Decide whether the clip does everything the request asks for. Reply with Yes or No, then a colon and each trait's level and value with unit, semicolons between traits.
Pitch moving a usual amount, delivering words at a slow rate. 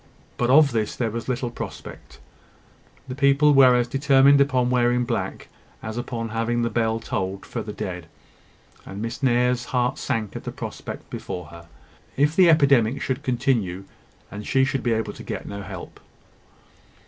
No: average, 3.3 semitones; average, 170 wpm